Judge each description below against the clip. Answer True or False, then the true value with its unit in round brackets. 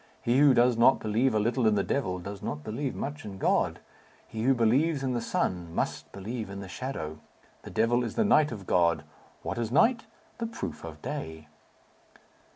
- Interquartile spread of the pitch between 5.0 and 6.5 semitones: True (5.3 semitones)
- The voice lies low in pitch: True (115 Hz)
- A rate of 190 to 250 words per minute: True (195 wpm)